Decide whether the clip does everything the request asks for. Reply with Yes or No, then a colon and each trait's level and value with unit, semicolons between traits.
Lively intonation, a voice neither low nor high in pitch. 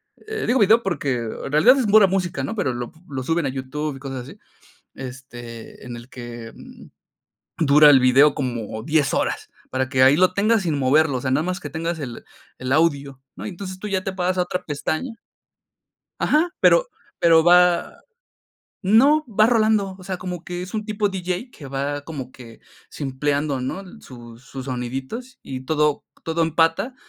Yes: wide, 6.4 semitones; medium, 155 Hz